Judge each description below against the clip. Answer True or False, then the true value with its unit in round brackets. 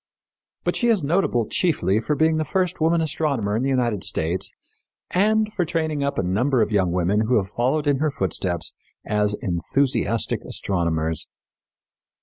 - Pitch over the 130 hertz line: False (125 Hz)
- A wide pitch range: True (8.1 semitones)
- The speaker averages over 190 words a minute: False (160 wpm)